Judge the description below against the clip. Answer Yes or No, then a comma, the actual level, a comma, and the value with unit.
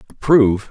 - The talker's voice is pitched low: Yes, low, 120 Hz